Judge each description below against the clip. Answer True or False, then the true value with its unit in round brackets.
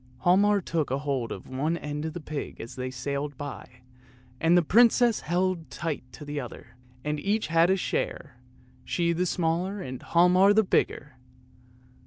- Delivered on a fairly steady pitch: False (4.4 semitones)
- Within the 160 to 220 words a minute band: True (165 wpm)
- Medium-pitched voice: True (165 Hz)